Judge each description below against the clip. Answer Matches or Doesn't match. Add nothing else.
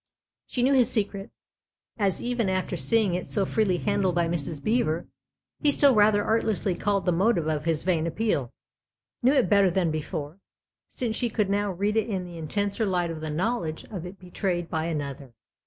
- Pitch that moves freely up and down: Doesn't match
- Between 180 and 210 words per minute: Matches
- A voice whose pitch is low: Doesn't match